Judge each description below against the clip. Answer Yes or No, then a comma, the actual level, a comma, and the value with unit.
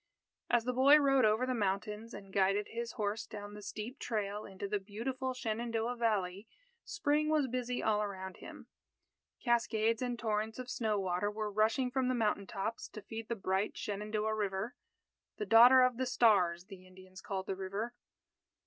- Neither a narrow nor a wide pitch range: Yes, average, 3.3 semitones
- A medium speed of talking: Yes, average, 175 wpm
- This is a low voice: No, high, 215 Hz